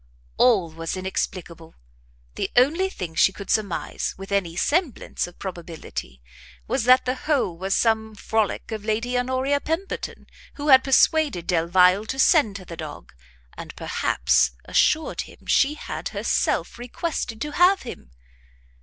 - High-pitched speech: Yes, high, 220 Hz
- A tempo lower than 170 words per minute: Yes, average, 145 wpm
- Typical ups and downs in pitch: No, wide, 7.1 semitones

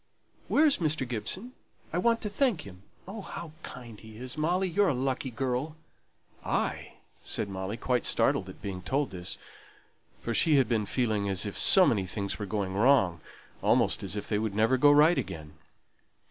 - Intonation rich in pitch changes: Yes, wide, 7.3 semitones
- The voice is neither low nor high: No, low, 125 Hz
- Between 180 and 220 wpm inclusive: Yes, average, 185 wpm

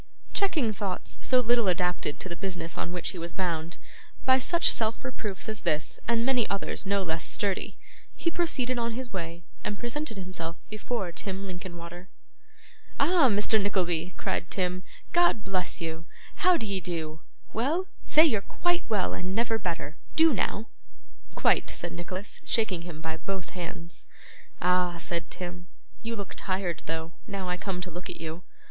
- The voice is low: No, high, 190 Hz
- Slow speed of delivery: No, average, 165 wpm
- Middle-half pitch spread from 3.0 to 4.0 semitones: No, average, 4.8 semitones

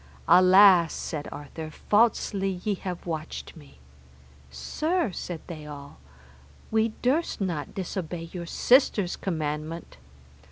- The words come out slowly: Yes, slow, 110 wpm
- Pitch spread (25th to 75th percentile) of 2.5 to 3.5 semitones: No, average, 4.6 semitones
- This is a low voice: No, medium, 175 Hz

